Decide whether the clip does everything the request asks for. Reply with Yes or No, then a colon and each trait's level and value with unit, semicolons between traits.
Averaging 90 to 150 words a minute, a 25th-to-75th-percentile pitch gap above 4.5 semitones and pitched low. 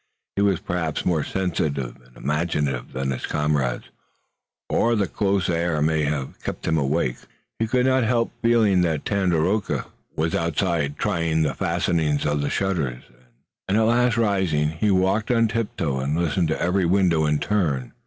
No: average, 165 wpm; average, 5.1 semitones; very low, 85 Hz